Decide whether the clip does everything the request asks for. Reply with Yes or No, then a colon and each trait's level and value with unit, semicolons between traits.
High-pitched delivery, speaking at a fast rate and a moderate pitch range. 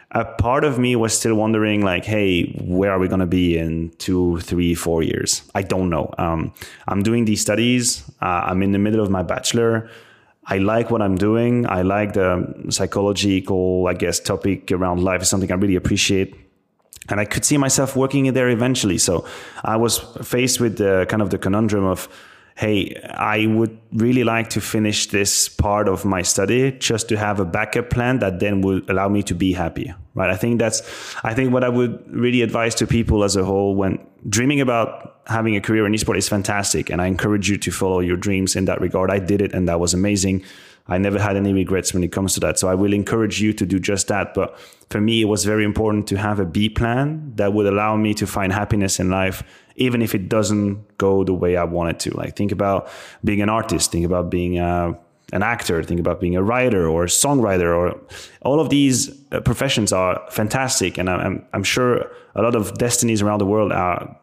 No: low, 100 Hz; fast, 220 wpm; average, 3.3 semitones